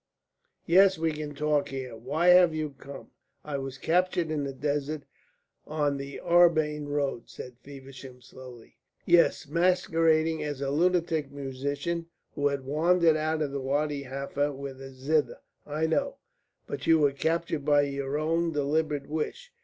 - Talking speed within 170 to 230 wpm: No, average, 150 wpm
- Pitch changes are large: No, average, 2.7 semitones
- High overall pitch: No, medium, 150 Hz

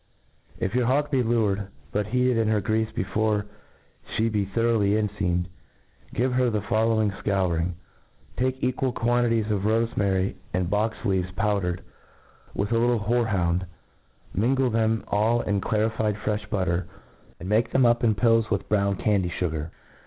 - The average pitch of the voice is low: Yes, low, 105 Hz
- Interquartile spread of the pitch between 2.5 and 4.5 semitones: Yes, average, 2.8 semitones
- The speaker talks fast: No, average, 150 wpm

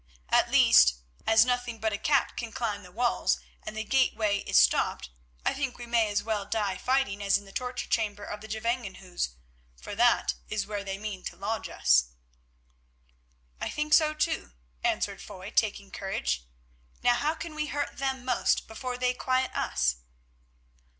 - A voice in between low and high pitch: No, high, 220 Hz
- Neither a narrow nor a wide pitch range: Yes, average, 4.0 semitones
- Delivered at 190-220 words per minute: No, average, 170 wpm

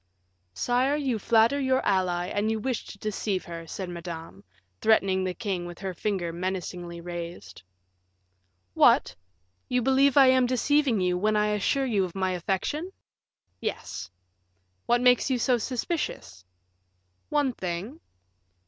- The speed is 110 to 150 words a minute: Yes, average, 140 wpm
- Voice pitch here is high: Yes, high, 205 Hz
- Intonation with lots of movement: Yes, wide, 6.0 semitones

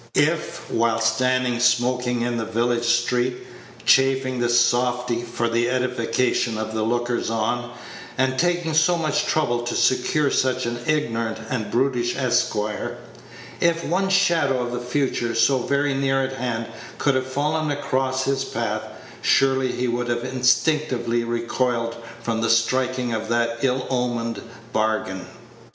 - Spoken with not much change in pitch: Yes, narrow, 2.1 semitones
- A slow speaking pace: No, average, 145 wpm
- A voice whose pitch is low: Yes, low, 125 Hz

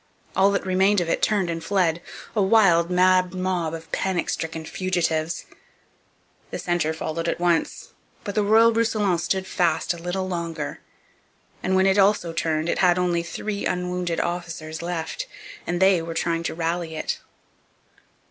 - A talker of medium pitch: Yes, medium, 175 Hz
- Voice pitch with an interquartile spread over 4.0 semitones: No, narrow, 2.4 semitones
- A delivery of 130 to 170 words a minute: Yes, average, 160 wpm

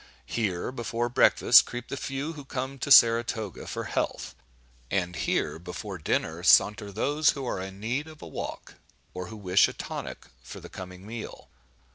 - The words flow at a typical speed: Yes, average, 170 wpm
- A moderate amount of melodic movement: No, wide, 5.8 semitones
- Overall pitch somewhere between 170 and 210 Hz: No, low, 110 Hz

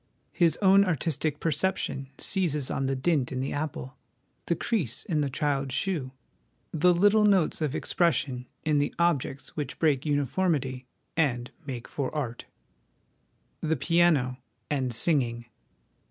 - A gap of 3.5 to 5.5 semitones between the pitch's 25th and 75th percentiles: Yes, average, 4.4 semitones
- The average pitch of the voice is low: No, medium, 145 Hz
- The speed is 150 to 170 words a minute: No, slow, 135 wpm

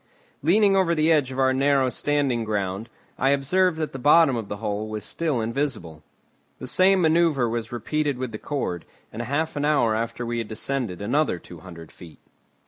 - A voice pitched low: Yes, low, 130 Hz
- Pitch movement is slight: No, wide, 5.6 semitones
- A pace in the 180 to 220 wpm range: Yes, average, 190 wpm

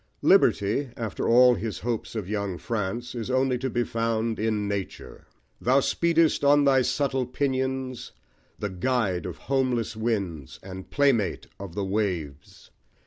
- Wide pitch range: No, average, 4.4 semitones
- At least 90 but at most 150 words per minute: Yes, average, 140 wpm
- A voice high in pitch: No, low, 115 Hz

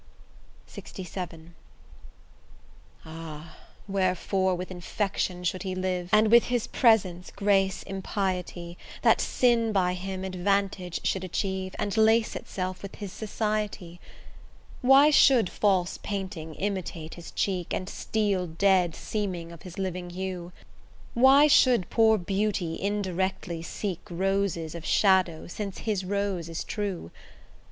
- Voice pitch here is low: No, high, 190 Hz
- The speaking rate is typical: No, slow, 120 wpm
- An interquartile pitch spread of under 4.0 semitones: Yes, narrow, 2.5 semitones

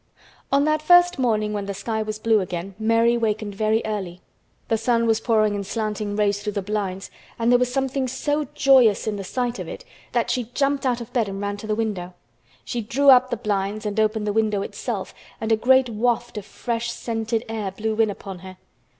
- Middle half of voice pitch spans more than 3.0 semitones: No, average, 2.7 semitones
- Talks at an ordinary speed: No, fast, 215 wpm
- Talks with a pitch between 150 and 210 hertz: No, high, 220 Hz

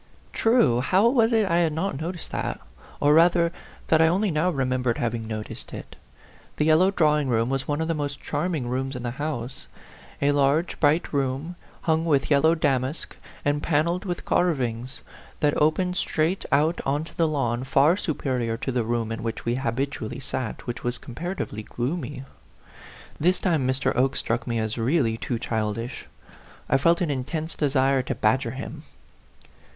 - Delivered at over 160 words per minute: Yes, average, 175 wpm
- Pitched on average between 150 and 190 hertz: No, medium, 140 Hz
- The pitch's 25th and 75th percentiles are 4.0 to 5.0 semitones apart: Yes, average, 4.6 semitones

